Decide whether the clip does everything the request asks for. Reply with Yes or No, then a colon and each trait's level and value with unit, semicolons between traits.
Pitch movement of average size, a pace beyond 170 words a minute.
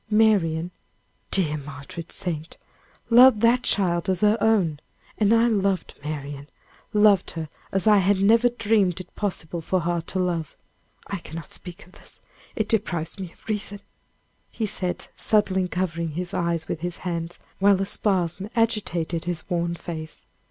No: average, 3.8 semitones; average, 155 wpm